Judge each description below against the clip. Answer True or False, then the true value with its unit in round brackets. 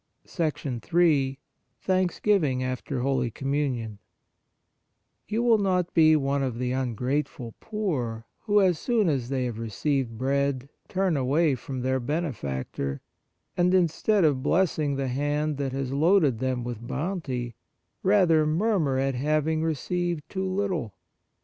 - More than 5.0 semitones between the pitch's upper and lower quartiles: True (5.4 semitones)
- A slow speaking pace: True (130 wpm)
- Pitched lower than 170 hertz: True (140 Hz)